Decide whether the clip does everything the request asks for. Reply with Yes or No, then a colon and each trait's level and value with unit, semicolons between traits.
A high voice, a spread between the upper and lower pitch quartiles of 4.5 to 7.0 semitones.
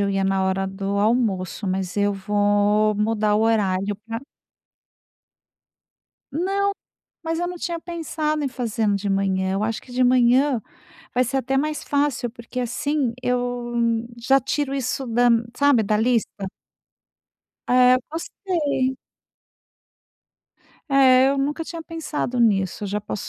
Yes: high, 245 Hz; average, 5.1 semitones